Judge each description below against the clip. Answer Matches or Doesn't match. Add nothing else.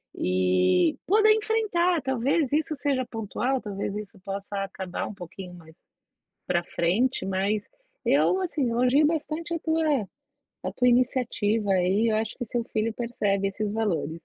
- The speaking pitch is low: Doesn't match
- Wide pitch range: Matches